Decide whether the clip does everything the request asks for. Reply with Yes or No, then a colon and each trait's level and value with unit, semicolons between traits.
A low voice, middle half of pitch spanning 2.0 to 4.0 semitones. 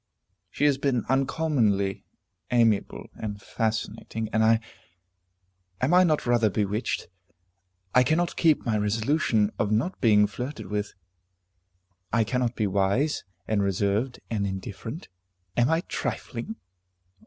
No: low, 115 Hz; average, 4.5 semitones